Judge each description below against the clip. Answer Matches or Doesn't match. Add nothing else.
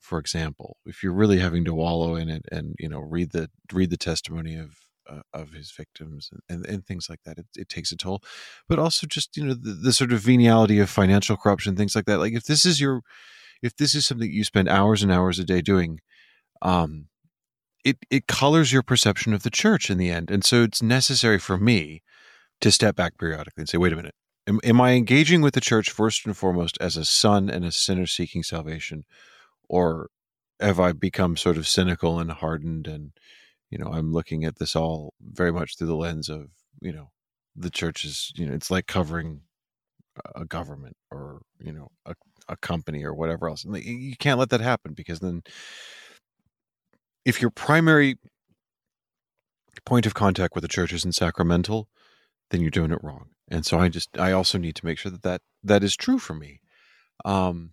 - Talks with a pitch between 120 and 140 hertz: Doesn't match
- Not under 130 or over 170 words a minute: Doesn't match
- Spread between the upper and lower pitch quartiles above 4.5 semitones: Matches